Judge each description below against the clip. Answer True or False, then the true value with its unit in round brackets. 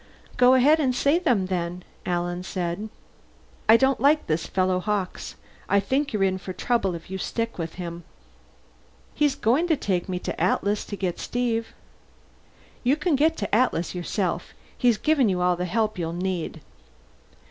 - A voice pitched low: False (200 Hz)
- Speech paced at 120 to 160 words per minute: False (180 wpm)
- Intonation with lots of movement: True (5.8 semitones)